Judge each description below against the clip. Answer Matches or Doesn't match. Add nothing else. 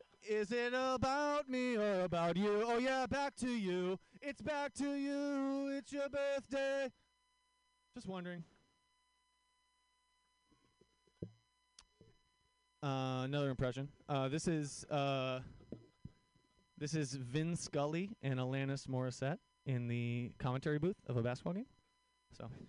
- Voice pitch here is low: Doesn't match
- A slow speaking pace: Matches